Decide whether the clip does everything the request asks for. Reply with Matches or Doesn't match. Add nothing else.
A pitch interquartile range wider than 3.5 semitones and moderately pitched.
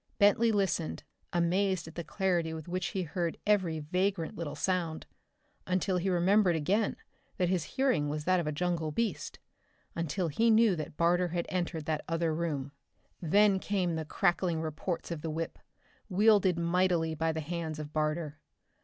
Doesn't match